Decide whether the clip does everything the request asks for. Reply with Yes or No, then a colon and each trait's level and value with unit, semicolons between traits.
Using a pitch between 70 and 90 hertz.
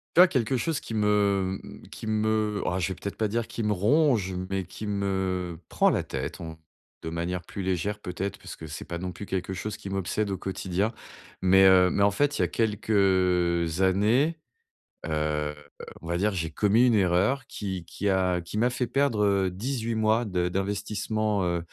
No: low, 100 Hz